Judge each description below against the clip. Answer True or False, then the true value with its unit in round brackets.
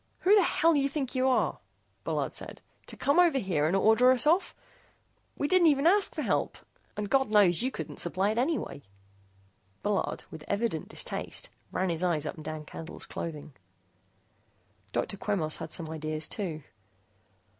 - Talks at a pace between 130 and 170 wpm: True (165 wpm)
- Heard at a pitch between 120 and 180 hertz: False (205 Hz)